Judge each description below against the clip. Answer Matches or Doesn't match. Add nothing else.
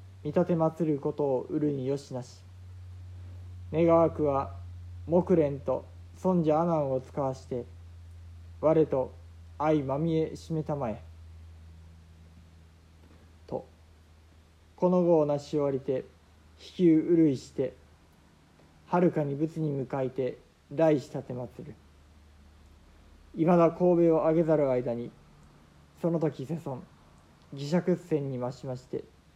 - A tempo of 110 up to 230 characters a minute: Matches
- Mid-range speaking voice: Doesn't match